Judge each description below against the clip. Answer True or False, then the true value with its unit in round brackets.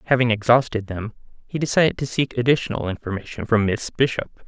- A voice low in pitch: True (115 Hz)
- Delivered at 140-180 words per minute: True (160 wpm)